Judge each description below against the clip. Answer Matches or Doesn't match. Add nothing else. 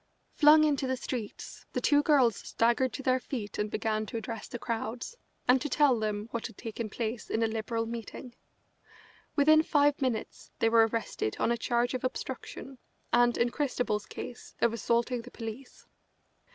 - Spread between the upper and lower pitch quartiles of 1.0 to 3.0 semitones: Matches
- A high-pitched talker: Matches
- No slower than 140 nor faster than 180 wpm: Matches